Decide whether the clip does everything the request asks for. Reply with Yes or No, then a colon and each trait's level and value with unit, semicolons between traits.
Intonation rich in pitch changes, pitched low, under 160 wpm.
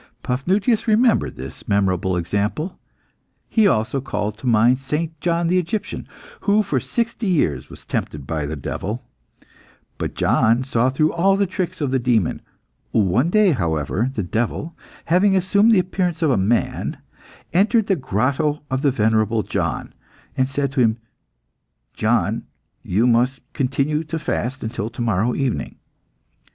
Yes: wide, 7.8 semitones; low, 130 Hz; average, 150 wpm